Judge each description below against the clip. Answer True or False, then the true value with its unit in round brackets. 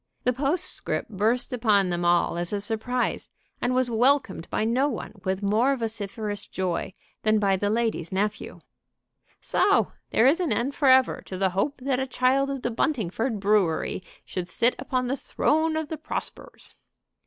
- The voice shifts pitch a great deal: False (4.8 semitones)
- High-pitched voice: True (230 Hz)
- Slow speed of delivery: False (165 wpm)